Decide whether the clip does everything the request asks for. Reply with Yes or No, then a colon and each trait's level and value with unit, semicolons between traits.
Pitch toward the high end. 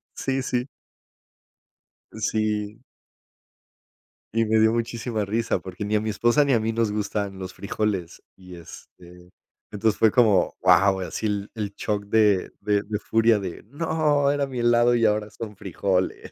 No: low, 105 Hz